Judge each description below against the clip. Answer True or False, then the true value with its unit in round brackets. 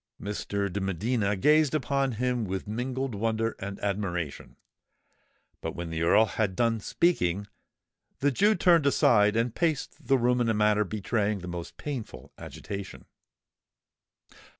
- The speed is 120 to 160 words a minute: True (140 wpm)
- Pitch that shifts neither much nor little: True (4.3 semitones)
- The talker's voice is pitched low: True (110 Hz)